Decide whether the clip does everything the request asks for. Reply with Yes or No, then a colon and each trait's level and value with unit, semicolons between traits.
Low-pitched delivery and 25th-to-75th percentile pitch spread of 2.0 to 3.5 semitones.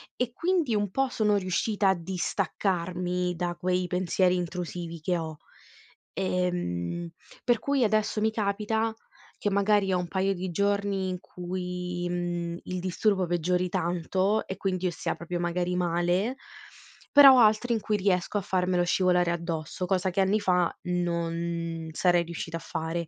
No: medium, 180 Hz; narrow, 2.5 semitones